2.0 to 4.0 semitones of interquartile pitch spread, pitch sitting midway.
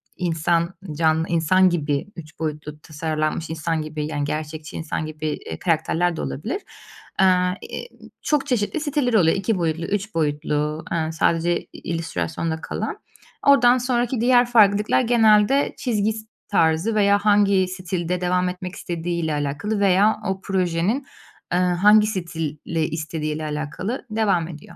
No: average, 4.6 semitones; medium, 175 Hz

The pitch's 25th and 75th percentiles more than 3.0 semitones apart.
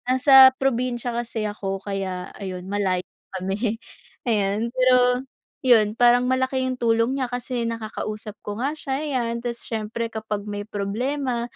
Yes: average, 3.4 semitones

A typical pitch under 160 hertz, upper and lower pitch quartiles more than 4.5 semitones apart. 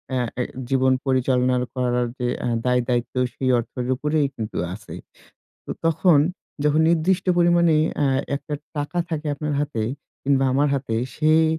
No: medium, 140 Hz; average, 3.7 semitones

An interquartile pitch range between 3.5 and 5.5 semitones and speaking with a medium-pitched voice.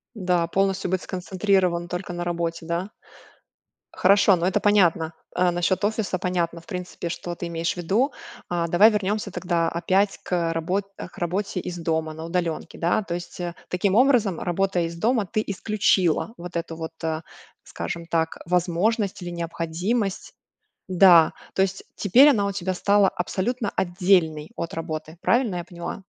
No: average, 2.7 semitones; medium, 180 Hz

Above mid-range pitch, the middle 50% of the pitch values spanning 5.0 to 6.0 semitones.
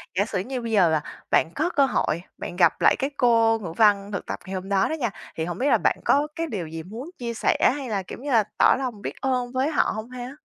Yes: high, 225 Hz; average, 5.3 semitones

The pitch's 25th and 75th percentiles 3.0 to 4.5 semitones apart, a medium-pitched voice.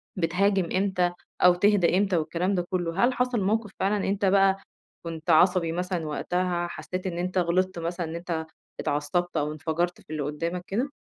No: narrow, 2.4 semitones; medium, 180 Hz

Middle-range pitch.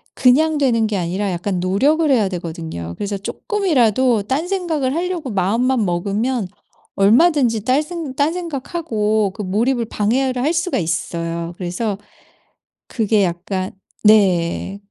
No: high, 220 Hz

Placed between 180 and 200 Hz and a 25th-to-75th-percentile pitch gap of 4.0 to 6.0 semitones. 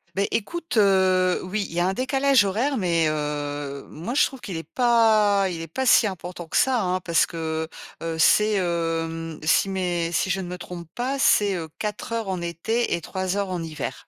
Yes: medium, 185 Hz; average, 4.4 semitones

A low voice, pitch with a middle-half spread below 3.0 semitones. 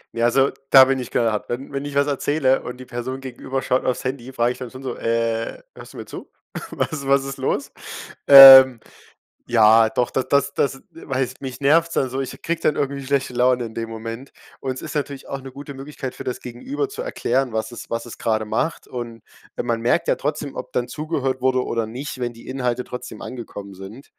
Yes: low, 130 Hz; narrow, 2.5 semitones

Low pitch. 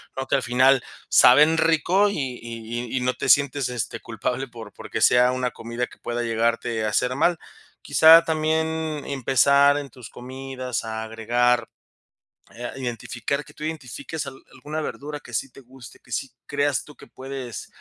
Yes: low, 130 Hz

